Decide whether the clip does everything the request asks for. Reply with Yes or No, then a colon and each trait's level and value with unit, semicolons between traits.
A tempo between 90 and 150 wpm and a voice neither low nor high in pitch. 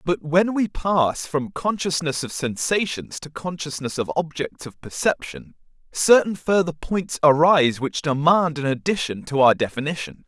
Yes: average, 145 wpm; medium, 160 Hz